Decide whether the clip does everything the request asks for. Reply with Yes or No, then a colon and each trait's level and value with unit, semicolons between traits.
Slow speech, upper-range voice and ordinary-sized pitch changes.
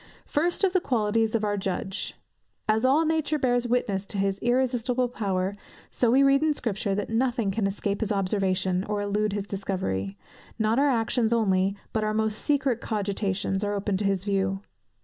No: average, 180 wpm; high, 215 Hz; average, 3.8 semitones